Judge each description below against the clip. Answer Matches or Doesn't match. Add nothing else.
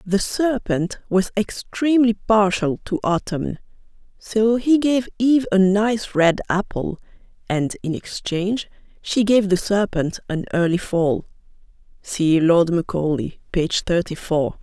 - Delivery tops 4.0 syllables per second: Doesn't match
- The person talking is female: Matches